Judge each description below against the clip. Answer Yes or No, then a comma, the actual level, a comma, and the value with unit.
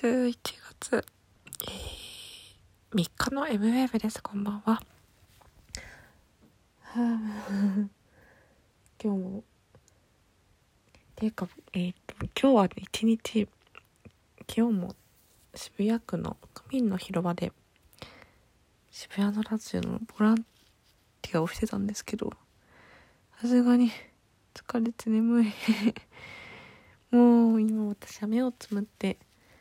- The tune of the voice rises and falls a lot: No, narrow, 2.6 semitones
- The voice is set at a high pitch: Yes, high, 215 Hz